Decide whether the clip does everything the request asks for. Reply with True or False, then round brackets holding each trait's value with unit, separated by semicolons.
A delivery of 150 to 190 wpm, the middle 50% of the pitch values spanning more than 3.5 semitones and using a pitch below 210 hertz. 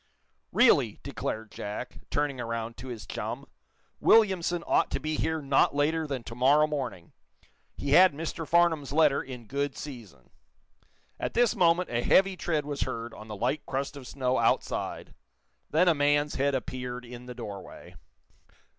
True (160 wpm; 4.2 semitones; 140 Hz)